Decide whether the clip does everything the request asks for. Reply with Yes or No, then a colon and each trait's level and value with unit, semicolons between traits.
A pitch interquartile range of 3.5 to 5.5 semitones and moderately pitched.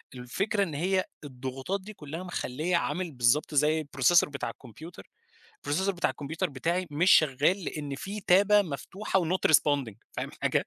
Yes: average, 5.0 semitones; medium, 160 Hz